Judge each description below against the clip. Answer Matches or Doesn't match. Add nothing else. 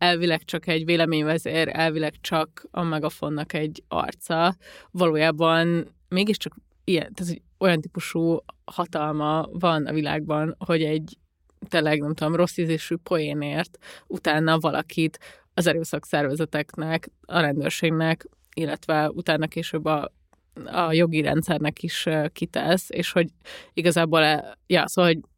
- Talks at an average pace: Matches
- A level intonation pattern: Matches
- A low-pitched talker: Doesn't match